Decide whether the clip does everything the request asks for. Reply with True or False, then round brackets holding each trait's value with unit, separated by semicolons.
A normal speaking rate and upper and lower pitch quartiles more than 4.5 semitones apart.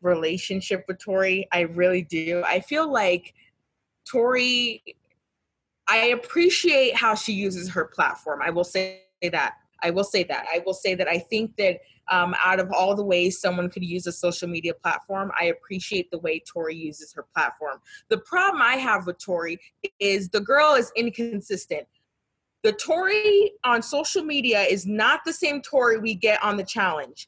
True (175 wpm; 5.4 semitones)